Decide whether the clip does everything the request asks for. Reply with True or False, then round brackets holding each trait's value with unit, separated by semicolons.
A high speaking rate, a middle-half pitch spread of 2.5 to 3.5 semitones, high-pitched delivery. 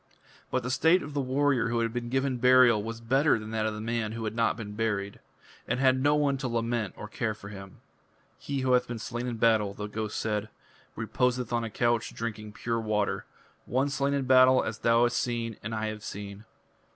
False (220 wpm; 2.9 semitones; 115 Hz)